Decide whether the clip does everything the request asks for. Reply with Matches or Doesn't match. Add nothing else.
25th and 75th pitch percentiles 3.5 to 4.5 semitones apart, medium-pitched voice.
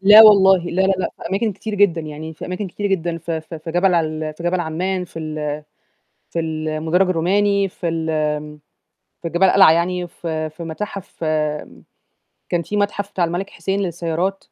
Doesn't match